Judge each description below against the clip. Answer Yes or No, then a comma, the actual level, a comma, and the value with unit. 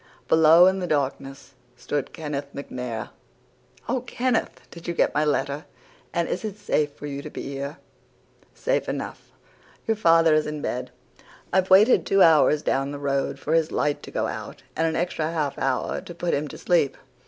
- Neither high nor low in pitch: Yes, medium, 155 Hz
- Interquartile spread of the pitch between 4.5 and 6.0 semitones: No, average, 3.6 semitones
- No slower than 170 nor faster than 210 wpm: Yes, average, 185 wpm